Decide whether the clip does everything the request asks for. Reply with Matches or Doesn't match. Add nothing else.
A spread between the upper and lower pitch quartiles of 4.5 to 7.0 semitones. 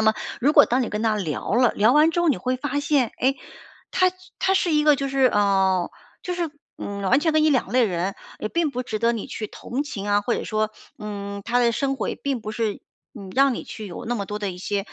Matches